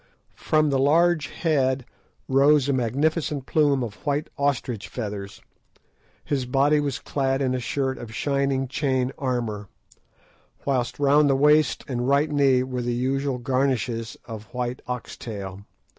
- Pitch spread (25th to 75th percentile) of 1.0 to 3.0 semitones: Yes, narrow, 2.6 semitones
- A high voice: No, low, 135 Hz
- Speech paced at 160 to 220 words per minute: No, average, 145 wpm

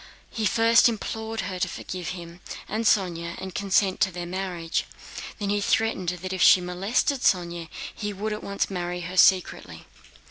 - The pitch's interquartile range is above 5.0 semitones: No, average, 2.7 semitones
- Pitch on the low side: No, high, 190 Hz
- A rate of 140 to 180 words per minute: Yes, average, 170 wpm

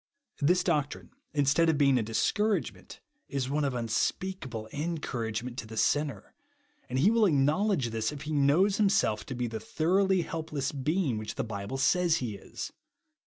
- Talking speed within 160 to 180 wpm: Yes, average, 170 wpm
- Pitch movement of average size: No, wide, 5.7 semitones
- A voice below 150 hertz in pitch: Yes, medium, 140 Hz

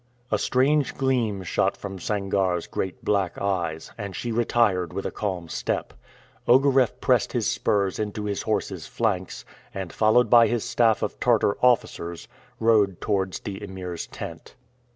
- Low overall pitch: Yes, low, 100 Hz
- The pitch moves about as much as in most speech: Yes, average, 3.5 semitones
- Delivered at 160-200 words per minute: No, average, 150 wpm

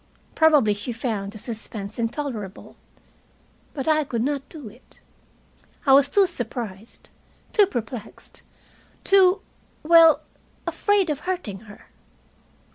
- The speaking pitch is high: Yes, very high, 260 Hz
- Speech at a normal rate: No, slow, 115 wpm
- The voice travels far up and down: Yes, wide, 6.4 semitones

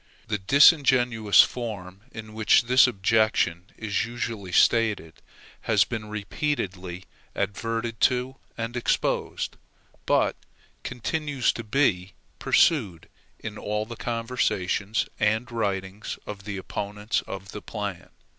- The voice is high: No, low, 110 Hz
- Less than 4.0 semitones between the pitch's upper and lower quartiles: Yes, average, 3.2 semitones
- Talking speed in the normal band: No, slow, 110 wpm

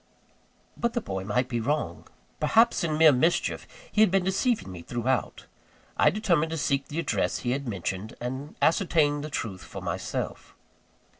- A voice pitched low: No, medium, 145 Hz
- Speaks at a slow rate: No, average, 165 wpm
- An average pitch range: No, wide, 6.0 semitones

